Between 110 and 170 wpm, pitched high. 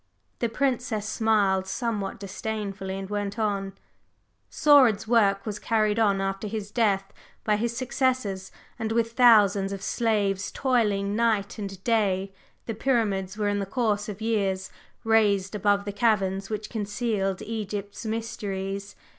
Yes: average, 140 wpm; high, 210 Hz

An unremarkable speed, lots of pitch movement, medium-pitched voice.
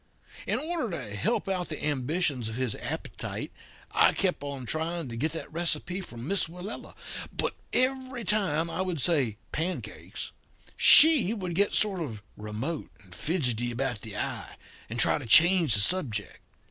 Yes: average, 160 wpm; wide, 7.3 semitones; medium, 160 Hz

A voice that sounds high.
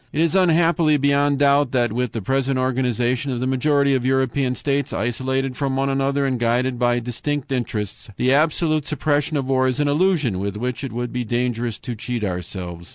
No: low, 130 Hz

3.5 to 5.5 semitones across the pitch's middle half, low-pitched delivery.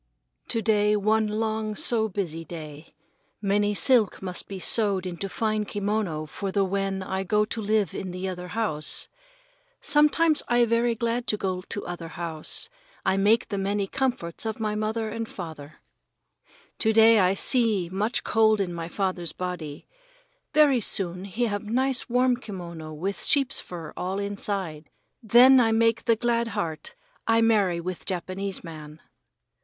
No: average, 3.8 semitones; high, 205 Hz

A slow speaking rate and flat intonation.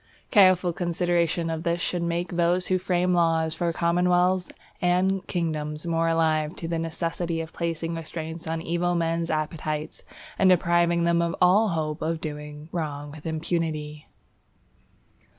No: average, 145 wpm; narrow, 1.6 semitones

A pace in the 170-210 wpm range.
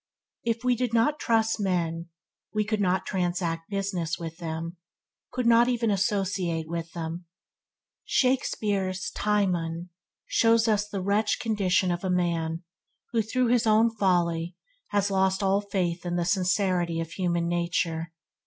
No: average, 145 wpm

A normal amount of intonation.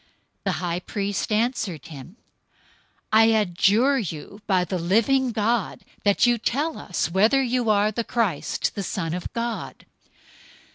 Yes: average, 4.4 semitones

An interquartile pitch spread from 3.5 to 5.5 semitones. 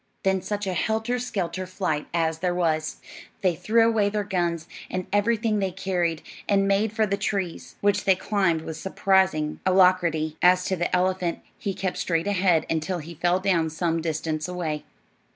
No: average, 3.1 semitones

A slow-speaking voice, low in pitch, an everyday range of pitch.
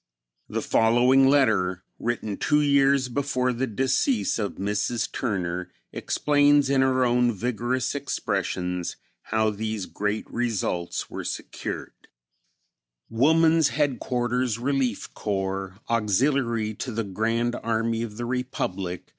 Yes: slow, 115 wpm; low, 120 Hz; average, 4.1 semitones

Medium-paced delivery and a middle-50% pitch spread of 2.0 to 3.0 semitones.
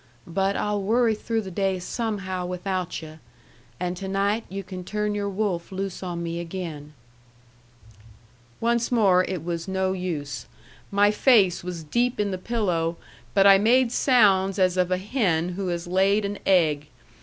Yes: average, 165 wpm; average, 2.7 semitones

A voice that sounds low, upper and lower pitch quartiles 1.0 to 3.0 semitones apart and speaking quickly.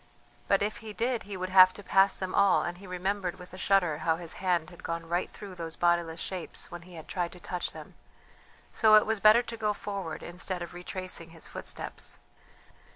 No: medium, 185 Hz; narrow, 2.5 semitones; fast, 215 wpm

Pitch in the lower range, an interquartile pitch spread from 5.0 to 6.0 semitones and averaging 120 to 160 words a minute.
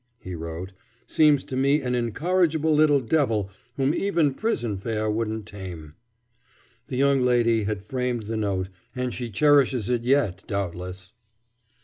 Yes: low, 120 Hz; wide, 5.5 semitones; average, 140 wpm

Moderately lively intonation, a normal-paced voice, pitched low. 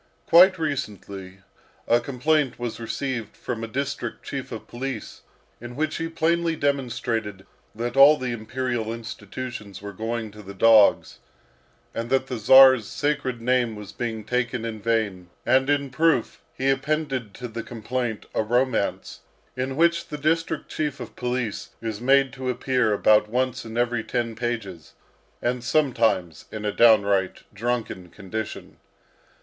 Yes: average, 3.4 semitones; average, 145 wpm; low, 120 Hz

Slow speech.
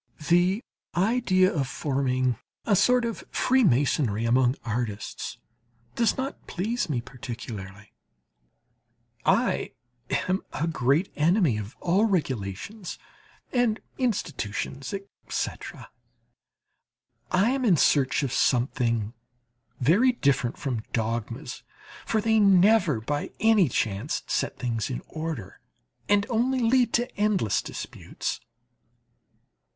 Yes: slow, 105 wpm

